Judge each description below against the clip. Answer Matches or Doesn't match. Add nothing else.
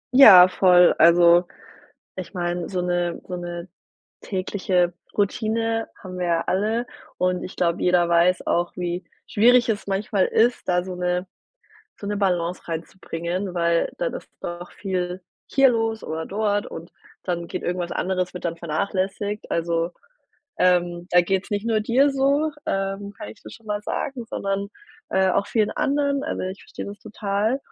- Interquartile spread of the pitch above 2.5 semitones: Matches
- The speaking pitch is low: Doesn't match